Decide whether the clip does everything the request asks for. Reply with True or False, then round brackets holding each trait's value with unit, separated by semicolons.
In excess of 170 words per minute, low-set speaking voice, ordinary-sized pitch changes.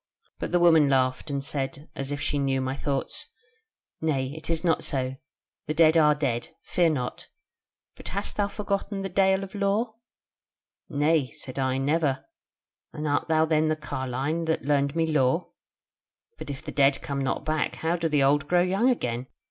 False (180 wpm; 150 Hz; 3.5 semitones)